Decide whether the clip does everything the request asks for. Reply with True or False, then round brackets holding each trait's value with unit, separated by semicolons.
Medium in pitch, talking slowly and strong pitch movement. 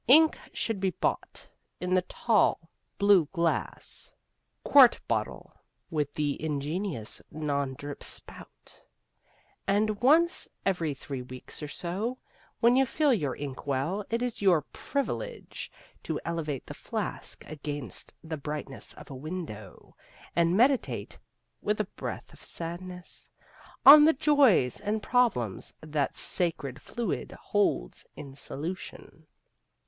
True (170 Hz; 125 wpm; 7.0 semitones)